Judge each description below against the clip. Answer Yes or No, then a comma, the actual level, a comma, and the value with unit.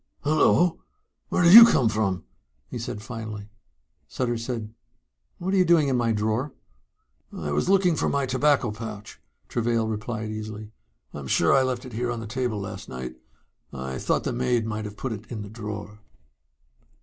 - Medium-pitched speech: No, low, 115 Hz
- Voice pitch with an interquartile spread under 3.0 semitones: No, average, 3.5 semitones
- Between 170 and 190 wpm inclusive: Yes, average, 175 wpm